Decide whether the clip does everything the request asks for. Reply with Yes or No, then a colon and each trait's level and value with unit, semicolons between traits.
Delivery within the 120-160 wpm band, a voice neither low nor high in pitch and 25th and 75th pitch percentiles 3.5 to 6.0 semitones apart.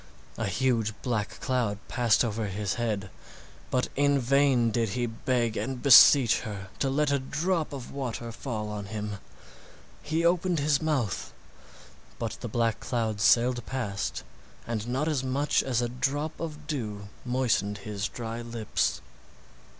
No: average, 150 wpm; low, 120 Hz; average, 4.1 semitones